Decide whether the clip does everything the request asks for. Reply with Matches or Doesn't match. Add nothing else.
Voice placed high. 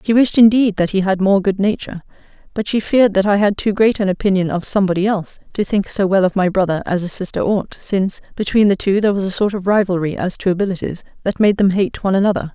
Matches